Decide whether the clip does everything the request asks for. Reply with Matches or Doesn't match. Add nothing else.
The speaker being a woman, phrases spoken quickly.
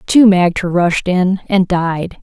Doesn't match